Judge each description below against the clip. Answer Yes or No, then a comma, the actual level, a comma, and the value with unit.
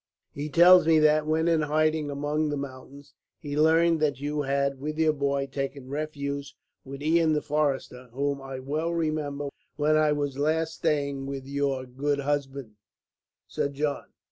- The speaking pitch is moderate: Yes, medium, 145 Hz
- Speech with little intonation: Yes, narrow, 1.8 semitones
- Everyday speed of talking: Yes, average, 165 wpm